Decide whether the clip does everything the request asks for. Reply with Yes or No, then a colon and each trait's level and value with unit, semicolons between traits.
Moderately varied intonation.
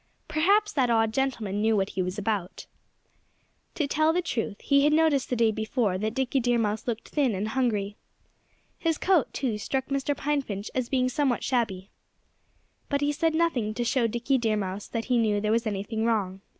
Yes: average, 4.7 semitones